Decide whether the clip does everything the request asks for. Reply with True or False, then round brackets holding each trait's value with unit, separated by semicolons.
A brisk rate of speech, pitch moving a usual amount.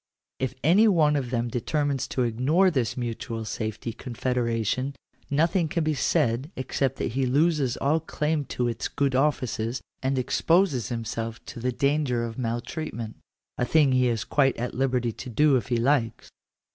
False (170 wpm; 3.9 semitones)